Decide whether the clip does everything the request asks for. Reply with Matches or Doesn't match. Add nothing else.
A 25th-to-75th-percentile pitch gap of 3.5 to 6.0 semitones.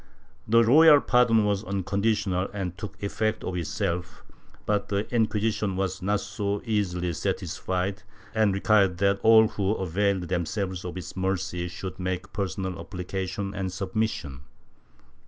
Doesn't match